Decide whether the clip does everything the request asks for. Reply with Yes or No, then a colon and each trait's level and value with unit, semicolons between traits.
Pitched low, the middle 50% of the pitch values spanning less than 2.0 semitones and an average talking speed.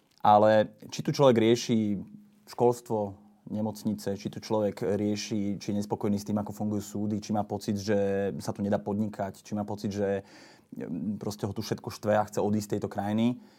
No: low, 105 Hz; narrow, 1.5 semitones; fast, 185 wpm